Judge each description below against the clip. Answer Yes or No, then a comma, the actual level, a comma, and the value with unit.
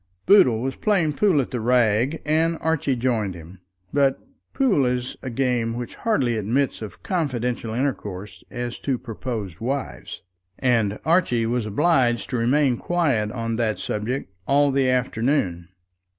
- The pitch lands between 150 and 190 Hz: No, low, 125 Hz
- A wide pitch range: No, average, 3.8 semitones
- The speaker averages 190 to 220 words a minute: No, average, 145 wpm